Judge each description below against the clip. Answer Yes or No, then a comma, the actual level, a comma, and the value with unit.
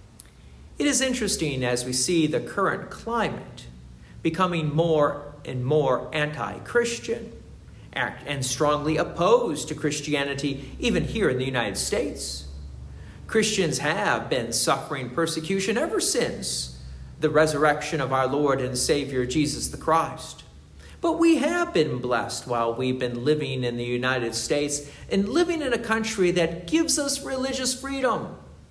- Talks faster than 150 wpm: No, average, 140 wpm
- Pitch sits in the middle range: Yes, medium, 150 Hz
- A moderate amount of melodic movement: No, wide, 7.5 semitones